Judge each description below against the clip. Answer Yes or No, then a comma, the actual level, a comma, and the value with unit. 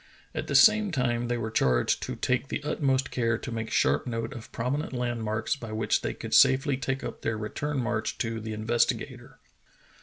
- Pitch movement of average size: Yes, average, 3.2 semitones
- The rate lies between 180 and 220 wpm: Yes, average, 190 wpm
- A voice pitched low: Yes, low, 120 Hz